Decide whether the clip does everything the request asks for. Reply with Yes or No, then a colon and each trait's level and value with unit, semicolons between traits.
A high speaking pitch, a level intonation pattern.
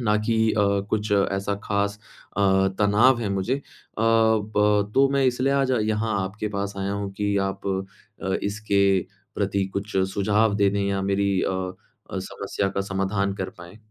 No: low, 100 Hz; narrow, 1.6 semitones